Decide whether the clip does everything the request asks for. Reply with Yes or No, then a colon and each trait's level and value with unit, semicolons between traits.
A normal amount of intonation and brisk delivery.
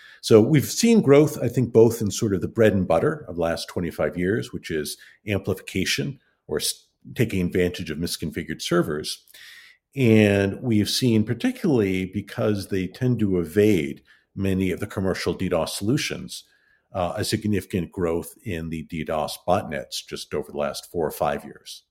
No: average, 4.2 semitones; average, 160 wpm